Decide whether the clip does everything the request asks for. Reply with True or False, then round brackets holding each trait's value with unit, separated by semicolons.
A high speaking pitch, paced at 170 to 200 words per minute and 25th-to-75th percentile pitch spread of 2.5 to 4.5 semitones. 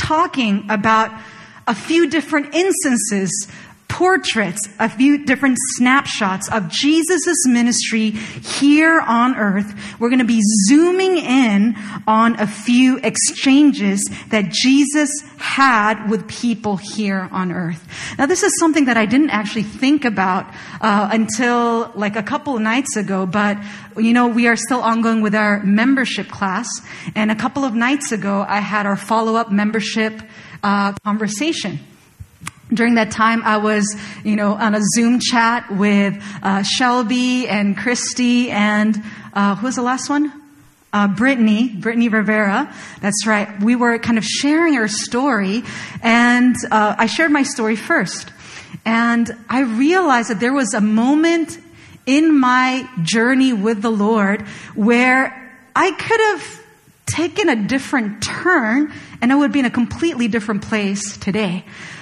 False (230 Hz; 150 wpm; 3.9 semitones)